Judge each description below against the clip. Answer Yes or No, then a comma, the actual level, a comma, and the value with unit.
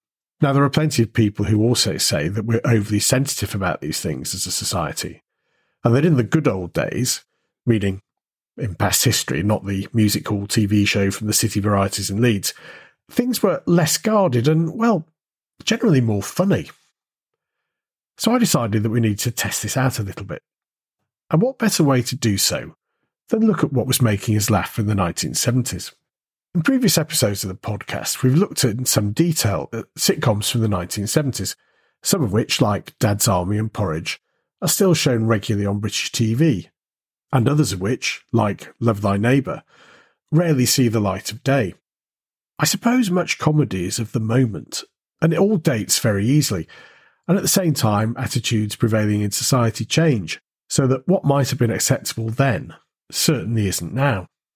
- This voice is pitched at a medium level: No, low, 115 Hz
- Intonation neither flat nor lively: No, wide, 6.5 semitones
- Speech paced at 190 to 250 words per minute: No, average, 180 wpm